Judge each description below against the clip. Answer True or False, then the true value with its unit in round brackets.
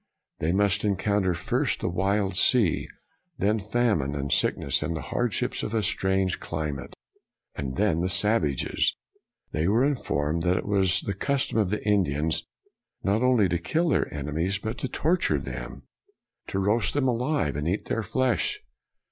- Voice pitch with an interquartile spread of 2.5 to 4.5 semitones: False (5.1 semitones)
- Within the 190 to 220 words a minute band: False (160 wpm)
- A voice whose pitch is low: True (95 Hz)